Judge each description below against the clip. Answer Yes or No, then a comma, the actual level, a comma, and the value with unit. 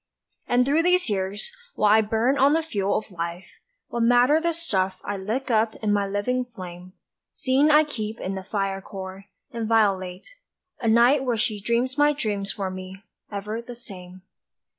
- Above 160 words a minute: Yes, average, 175 wpm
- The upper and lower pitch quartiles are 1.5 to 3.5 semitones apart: No, average, 4.4 semitones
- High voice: Yes, high, 215 Hz